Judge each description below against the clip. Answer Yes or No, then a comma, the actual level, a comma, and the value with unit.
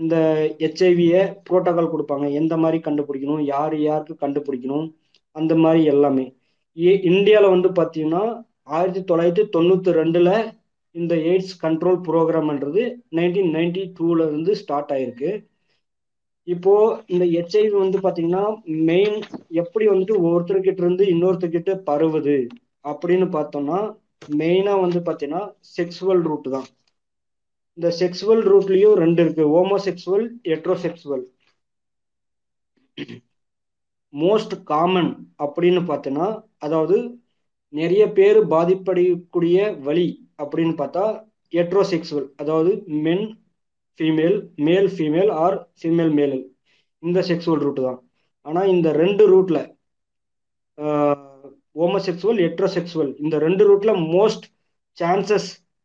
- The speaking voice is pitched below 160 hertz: No, medium, 170 Hz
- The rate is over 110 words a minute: No, average, 105 wpm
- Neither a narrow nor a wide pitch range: Yes, average, 4.0 semitones